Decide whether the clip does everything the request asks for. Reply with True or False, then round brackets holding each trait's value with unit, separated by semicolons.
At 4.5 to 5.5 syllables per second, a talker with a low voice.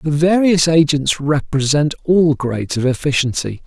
False (4.6 syllables/s; 150 Hz)